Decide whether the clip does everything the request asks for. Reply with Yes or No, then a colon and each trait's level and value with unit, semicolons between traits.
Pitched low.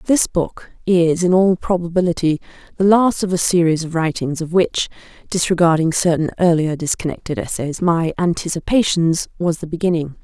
No: medium, 170 Hz